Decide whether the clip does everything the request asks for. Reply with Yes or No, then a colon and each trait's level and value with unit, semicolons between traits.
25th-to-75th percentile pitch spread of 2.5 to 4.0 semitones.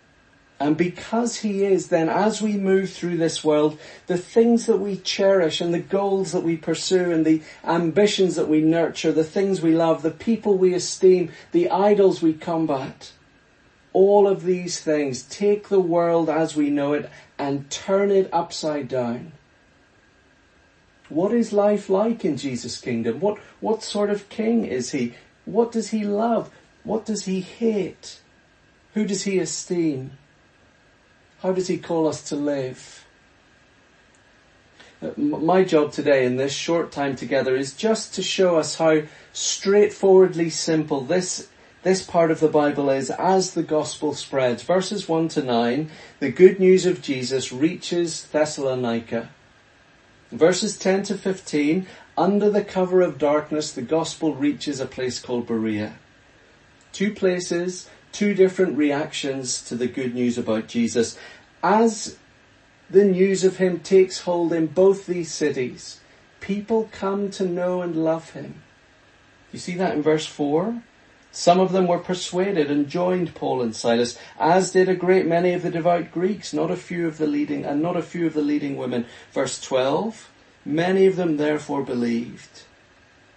No: average, 4.4 semitones